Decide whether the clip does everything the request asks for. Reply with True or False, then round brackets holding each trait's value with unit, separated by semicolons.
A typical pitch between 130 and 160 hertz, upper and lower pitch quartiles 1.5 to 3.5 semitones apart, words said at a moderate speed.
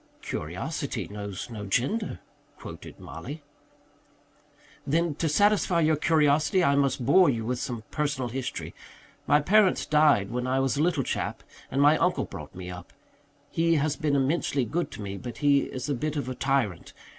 False (140 Hz; 4.1 semitones; 170 wpm)